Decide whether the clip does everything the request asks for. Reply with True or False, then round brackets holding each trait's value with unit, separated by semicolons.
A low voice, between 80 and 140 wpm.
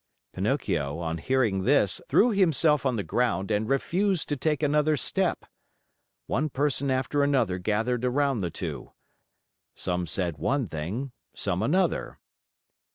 True (130 Hz; 135 wpm)